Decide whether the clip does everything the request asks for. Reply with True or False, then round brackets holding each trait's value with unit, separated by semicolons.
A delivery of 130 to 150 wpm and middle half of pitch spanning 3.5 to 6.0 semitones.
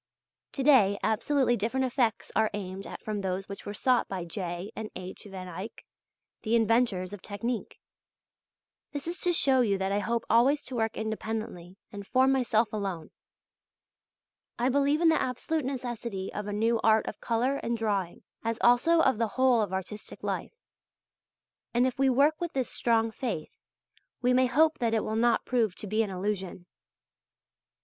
False (175 wpm; 4.1 semitones)